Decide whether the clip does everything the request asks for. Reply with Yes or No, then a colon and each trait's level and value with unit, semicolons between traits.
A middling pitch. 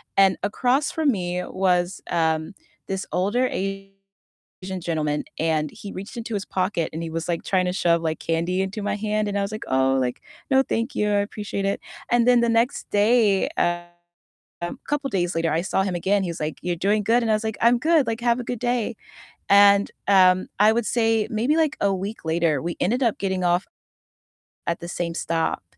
No: high, 195 Hz